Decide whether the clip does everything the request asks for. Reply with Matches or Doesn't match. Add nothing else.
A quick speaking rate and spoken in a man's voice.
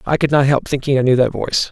Matches